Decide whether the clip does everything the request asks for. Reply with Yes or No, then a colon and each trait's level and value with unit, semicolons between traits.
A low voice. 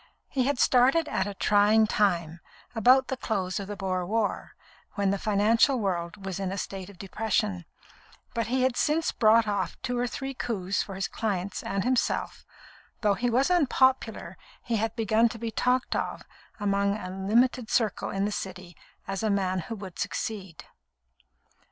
No: high, 210 Hz